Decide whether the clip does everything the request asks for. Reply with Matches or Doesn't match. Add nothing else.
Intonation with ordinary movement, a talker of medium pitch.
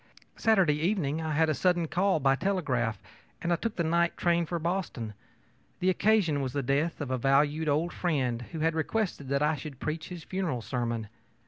Matches